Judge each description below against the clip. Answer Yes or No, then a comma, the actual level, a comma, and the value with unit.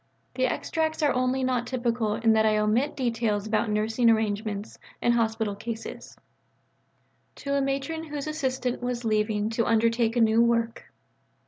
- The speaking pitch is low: No, high, 230 Hz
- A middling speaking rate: Yes, average, 150 wpm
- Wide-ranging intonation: No, average, 2.8 semitones